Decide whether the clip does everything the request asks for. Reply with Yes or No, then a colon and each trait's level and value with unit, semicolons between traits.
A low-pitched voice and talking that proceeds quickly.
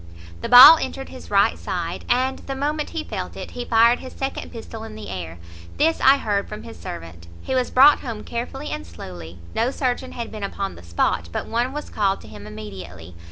No: high, 225 Hz; fast, 210 wpm